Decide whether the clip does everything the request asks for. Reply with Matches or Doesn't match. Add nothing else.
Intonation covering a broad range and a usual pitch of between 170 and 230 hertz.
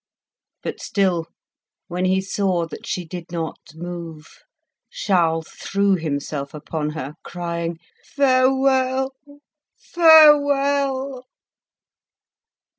Matches